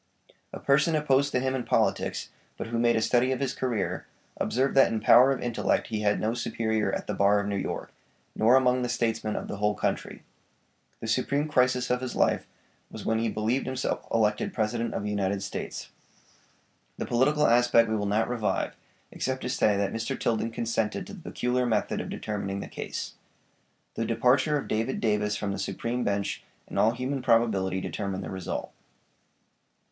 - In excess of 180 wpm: Yes, average, 190 wpm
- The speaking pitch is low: Yes, low, 115 Hz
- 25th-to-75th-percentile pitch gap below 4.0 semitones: Yes, average, 3.3 semitones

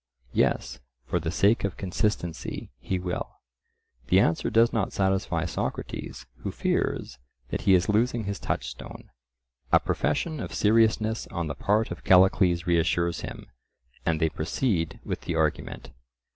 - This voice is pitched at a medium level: No, very low, 95 Hz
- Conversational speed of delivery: Yes, average, 145 wpm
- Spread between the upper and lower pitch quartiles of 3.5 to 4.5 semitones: Yes, average, 4.1 semitones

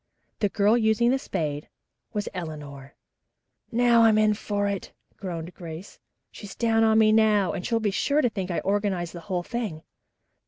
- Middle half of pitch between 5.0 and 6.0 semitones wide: No, average, 4.0 semitones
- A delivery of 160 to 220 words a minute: Yes, average, 170 wpm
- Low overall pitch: No, high, 205 Hz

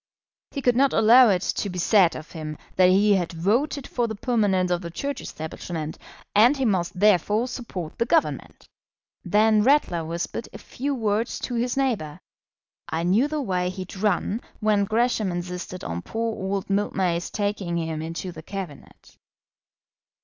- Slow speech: No, average, 165 wpm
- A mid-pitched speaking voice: No, high, 200 Hz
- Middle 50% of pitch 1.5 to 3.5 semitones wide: No, average, 4.7 semitones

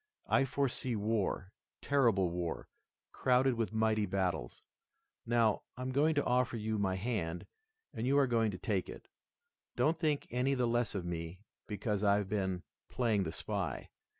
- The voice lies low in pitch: Yes, low, 110 Hz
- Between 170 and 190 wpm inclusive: No, average, 155 wpm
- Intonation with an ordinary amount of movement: Yes, average, 4.7 semitones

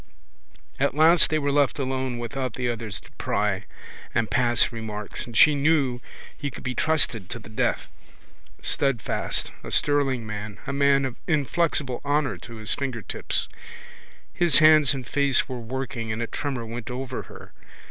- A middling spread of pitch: Yes, average, 3.4 semitones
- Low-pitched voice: Yes, low, 130 Hz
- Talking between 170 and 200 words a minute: No, average, 160 wpm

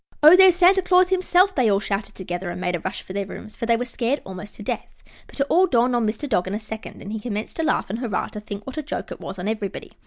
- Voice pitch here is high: Yes, high, 220 Hz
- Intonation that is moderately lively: No, wide, 6.9 semitones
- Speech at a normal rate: No, fast, 290 wpm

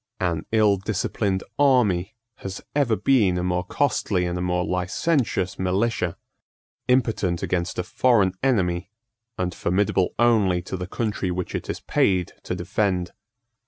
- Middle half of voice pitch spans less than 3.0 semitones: No, average, 3.5 semitones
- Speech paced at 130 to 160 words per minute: Yes, average, 140 wpm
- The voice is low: Yes, very low, 95 Hz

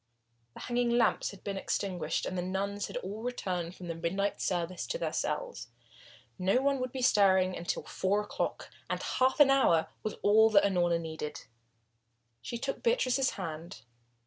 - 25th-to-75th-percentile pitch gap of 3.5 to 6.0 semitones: Yes, wide, 5.5 semitones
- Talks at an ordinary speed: Yes, average, 170 wpm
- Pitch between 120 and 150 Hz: No, high, 200 Hz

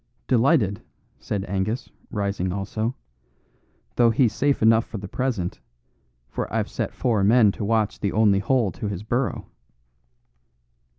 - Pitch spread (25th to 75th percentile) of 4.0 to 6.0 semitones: No, average, 3.1 semitones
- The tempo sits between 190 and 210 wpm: No, slow, 135 wpm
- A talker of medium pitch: No, low, 110 Hz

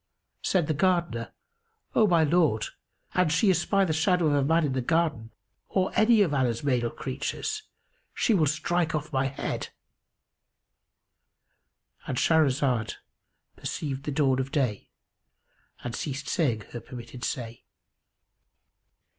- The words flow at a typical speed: No, slow, 130 wpm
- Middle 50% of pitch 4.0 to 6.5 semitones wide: Yes, average, 4.7 semitones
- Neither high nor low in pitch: Yes, medium, 145 Hz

